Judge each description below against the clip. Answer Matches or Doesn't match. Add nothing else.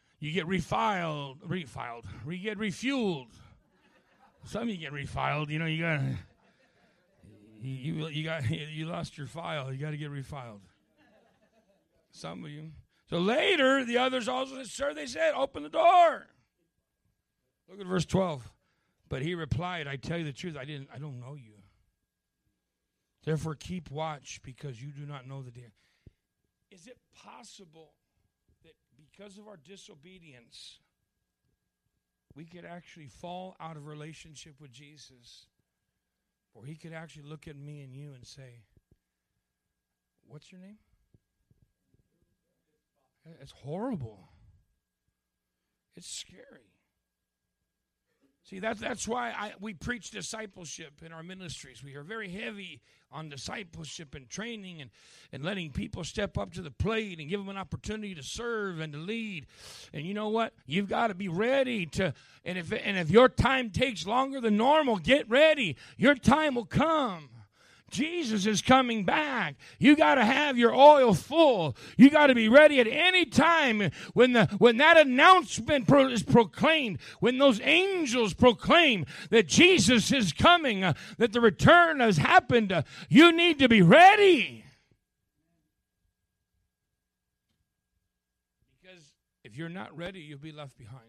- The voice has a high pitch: Doesn't match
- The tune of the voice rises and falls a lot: Matches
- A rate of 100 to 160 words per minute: Matches